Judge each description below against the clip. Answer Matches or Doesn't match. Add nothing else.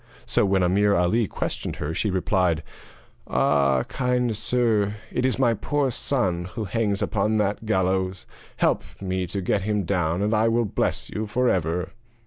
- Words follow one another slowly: Doesn't match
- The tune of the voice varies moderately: Matches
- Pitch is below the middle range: Matches